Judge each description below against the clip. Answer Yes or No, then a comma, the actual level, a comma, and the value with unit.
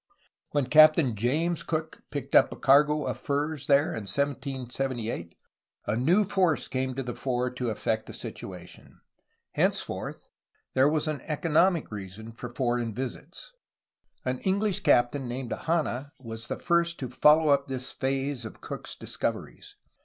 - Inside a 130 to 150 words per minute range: Yes, average, 145 wpm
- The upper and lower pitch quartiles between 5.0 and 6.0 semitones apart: No, average, 4.0 semitones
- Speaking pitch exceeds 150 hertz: No, low, 135 Hz